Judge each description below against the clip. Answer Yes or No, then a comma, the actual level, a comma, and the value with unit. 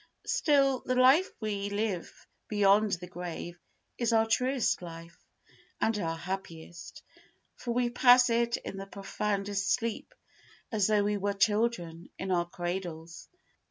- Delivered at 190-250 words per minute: No, slow, 135 wpm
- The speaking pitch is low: No, high, 205 Hz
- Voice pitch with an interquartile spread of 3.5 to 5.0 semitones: Yes, average, 4.6 semitones